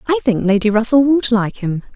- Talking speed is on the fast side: Yes, fast, 215 wpm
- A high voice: Yes, high, 235 Hz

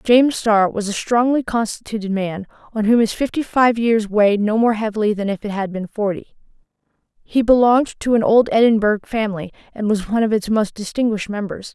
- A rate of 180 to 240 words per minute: Yes, average, 195 wpm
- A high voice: Yes, high, 215 Hz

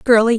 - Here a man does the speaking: No, female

